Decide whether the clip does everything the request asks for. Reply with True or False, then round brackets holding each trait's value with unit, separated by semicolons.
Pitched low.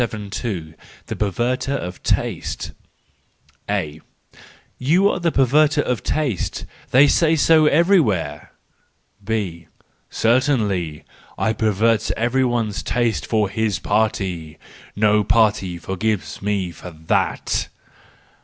True (110 Hz)